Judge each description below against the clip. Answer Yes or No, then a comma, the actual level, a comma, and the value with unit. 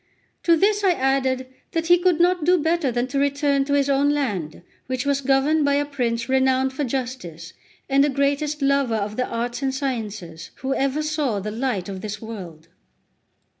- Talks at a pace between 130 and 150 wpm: No, average, 190 wpm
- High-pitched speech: Yes, very high, 270 Hz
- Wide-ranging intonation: No, average, 3.8 semitones